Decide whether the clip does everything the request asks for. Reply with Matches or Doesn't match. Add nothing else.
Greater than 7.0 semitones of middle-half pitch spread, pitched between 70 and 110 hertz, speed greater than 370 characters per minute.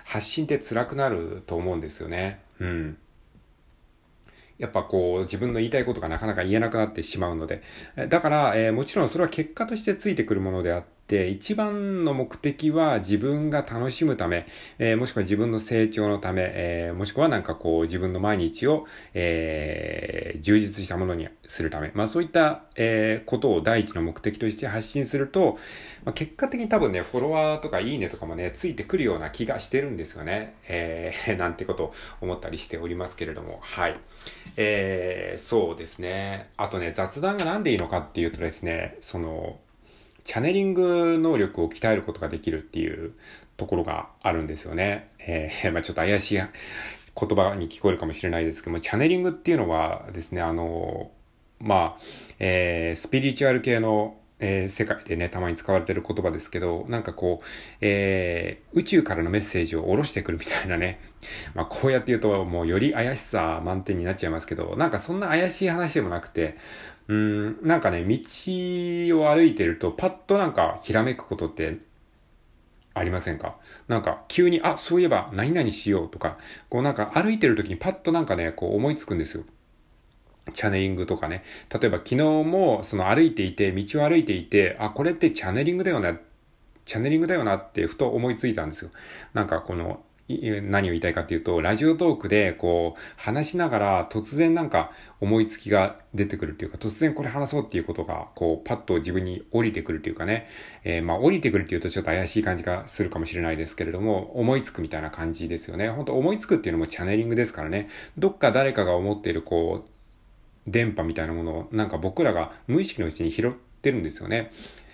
Matches